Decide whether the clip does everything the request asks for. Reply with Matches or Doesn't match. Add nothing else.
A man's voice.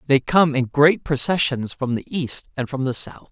Matches